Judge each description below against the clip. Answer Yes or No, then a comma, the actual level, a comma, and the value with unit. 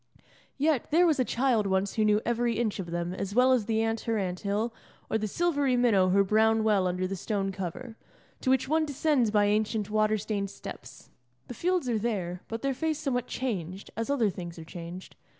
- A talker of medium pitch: No, high, 220 Hz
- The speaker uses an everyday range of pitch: Yes, average, 4.4 semitones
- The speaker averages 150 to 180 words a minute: No, fast, 205 wpm